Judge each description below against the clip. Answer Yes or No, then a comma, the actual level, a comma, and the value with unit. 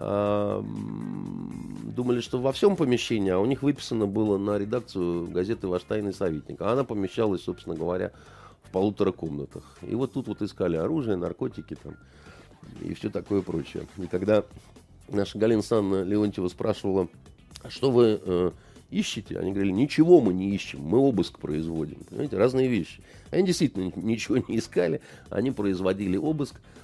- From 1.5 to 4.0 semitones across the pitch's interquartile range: No, average, 4.9 semitones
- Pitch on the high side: No, low, 105 Hz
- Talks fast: No, average, 150 wpm